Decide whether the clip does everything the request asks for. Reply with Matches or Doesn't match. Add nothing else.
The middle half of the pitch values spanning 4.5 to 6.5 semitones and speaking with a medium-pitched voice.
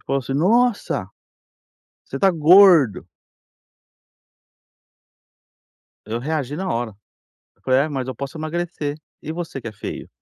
Matches